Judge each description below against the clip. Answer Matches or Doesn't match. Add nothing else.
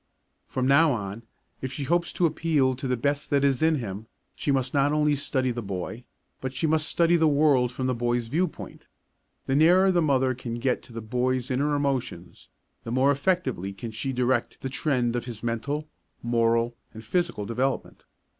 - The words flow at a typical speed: Matches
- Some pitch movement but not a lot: Matches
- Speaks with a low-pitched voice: Matches